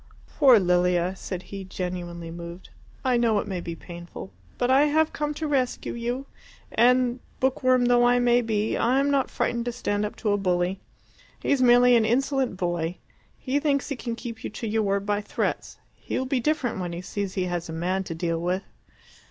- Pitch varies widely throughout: Yes, wide, 5.8 semitones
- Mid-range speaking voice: No, high, 220 Hz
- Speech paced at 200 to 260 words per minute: Yes, fast, 205 wpm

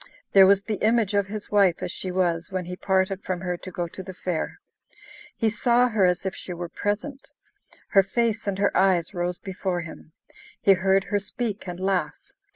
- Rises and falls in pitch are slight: Yes, narrow, 2.3 semitones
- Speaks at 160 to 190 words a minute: No, average, 200 wpm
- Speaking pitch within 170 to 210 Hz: Yes, high, 190 Hz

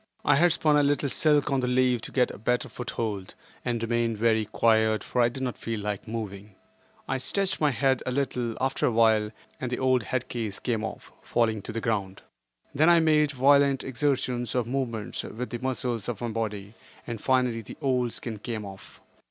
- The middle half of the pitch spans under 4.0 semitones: Yes, average, 3.1 semitones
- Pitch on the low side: Yes, low, 120 Hz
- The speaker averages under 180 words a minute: No, average, 200 wpm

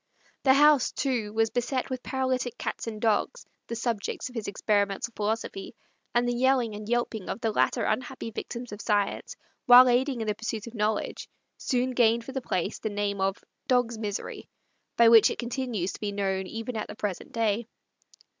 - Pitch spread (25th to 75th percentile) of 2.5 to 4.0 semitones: Yes, average, 2.9 semitones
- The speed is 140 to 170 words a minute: No, average, 185 wpm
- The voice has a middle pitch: No, high, 230 Hz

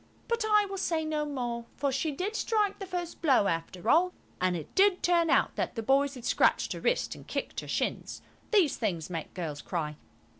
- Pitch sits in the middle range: No, very high, 290 Hz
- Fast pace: Yes, fast, 210 wpm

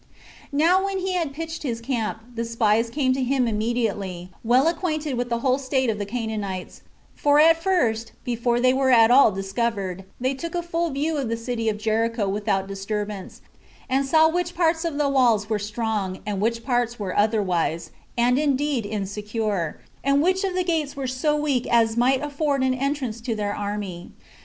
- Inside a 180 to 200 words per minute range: Yes, average, 190 wpm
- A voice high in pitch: Yes, high, 240 Hz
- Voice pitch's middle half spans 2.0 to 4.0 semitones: No, average, 5.1 semitones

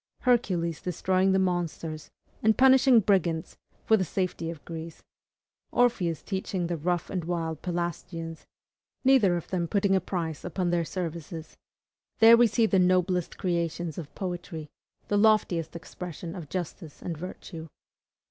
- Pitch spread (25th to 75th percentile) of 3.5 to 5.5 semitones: No, narrow, 2.5 semitones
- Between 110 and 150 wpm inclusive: Yes, average, 140 wpm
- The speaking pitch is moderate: Yes, medium, 175 Hz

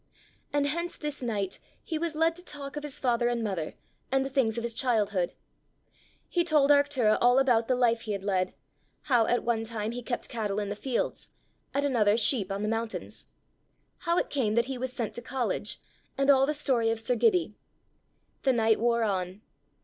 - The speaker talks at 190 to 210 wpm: Yes, average, 200 wpm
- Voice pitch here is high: Yes, high, 240 Hz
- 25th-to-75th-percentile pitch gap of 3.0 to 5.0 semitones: Yes, average, 4.0 semitones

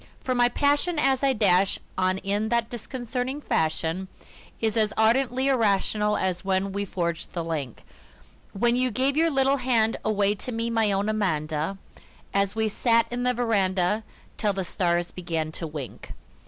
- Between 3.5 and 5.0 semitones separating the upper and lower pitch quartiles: Yes, average, 4.7 semitones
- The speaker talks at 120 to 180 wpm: Yes, average, 165 wpm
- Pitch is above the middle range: Yes, high, 210 Hz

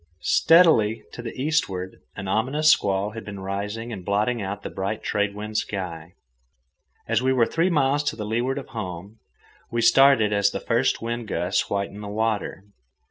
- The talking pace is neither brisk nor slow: Yes, average, 170 wpm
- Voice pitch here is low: Yes, low, 110 Hz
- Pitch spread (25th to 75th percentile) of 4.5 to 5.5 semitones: No, average, 3.4 semitones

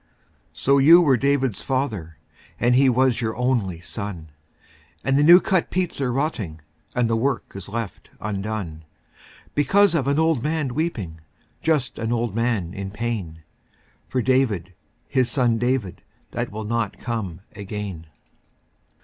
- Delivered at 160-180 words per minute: No, average, 145 wpm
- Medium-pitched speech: No, low, 120 Hz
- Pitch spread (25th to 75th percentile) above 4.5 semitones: Yes, average, 5.1 semitones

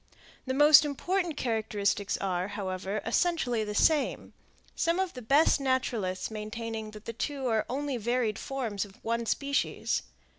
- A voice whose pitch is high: Yes, high, 235 Hz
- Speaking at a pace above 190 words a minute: No, average, 145 wpm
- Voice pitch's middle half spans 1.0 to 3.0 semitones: No, average, 4.8 semitones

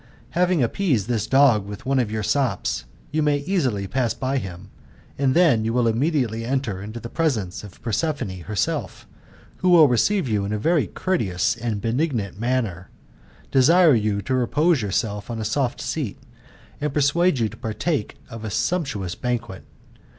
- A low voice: Yes, low, 120 Hz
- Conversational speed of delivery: Yes, average, 165 wpm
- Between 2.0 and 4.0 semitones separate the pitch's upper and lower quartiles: No, wide, 5.5 semitones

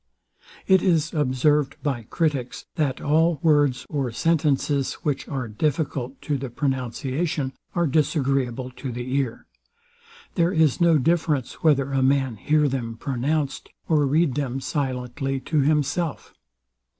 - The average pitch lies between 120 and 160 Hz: Yes, medium, 140 Hz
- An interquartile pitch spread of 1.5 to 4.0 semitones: Yes, average, 3.0 semitones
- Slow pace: Yes, slow, 130 wpm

